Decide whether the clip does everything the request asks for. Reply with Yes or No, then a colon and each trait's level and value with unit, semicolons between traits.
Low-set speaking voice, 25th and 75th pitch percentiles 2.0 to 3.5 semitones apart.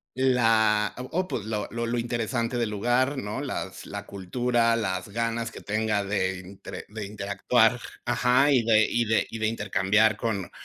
Yes: low, 110 Hz; narrow, 2.6 semitones